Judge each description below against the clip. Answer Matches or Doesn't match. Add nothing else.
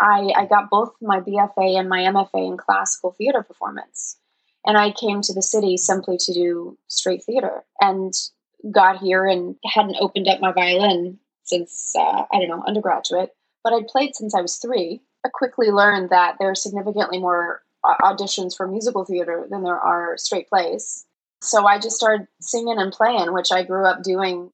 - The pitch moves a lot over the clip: Doesn't match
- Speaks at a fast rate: Doesn't match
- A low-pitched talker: Doesn't match